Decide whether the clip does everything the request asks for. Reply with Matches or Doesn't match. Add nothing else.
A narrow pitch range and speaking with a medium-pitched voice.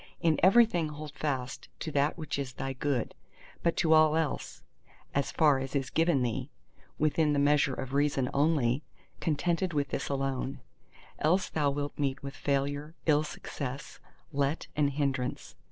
Matches